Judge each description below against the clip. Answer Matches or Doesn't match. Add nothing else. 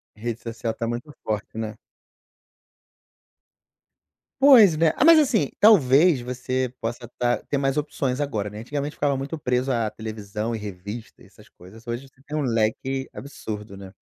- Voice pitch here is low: Matches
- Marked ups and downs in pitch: Doesn't match